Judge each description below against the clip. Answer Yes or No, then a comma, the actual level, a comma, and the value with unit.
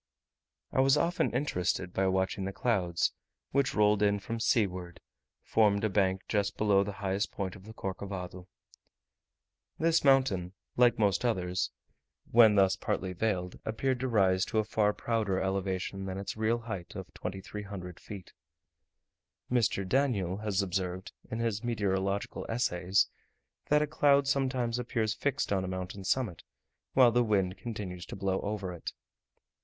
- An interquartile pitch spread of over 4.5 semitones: No, average, 3.6 semitones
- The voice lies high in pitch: No, low, 100 Hz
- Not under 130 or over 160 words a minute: Yes, average, 150 wpm